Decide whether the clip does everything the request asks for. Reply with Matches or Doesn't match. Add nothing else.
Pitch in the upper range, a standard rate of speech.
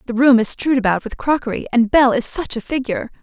Doesn't match